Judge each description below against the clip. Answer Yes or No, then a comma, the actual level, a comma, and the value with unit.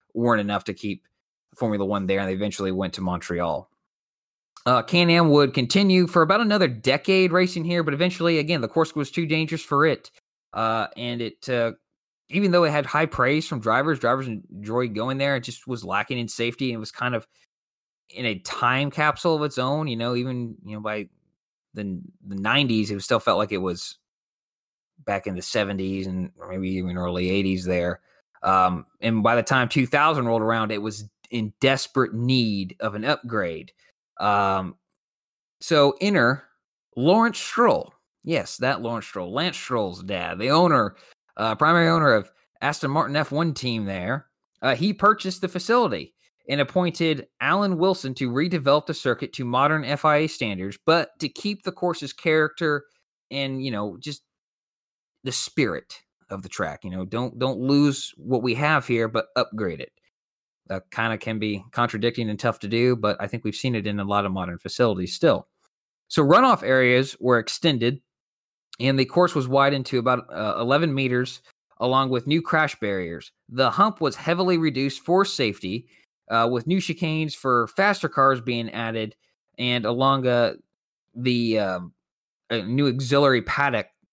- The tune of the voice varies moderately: No, wide, 5.9 semitones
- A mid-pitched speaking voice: No, low, 125 Hz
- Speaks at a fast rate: No, average, 175 wpm